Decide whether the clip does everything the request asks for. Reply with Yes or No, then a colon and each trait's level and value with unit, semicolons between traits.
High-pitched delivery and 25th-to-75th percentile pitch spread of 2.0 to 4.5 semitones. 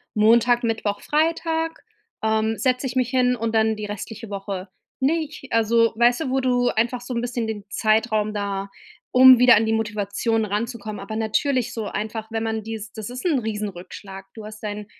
Yes: high, 225 Hz; average, 2.7 semitones